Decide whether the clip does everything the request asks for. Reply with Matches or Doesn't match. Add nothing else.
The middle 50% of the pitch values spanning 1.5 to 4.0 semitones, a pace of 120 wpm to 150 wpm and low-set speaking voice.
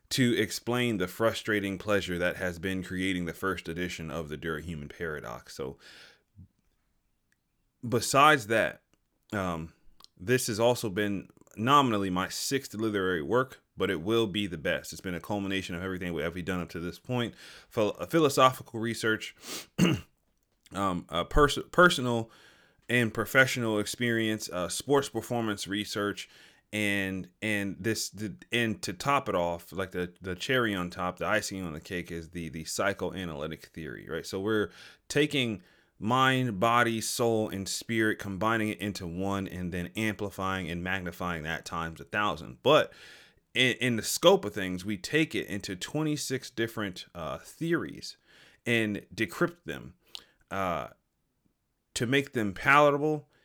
Doesn't match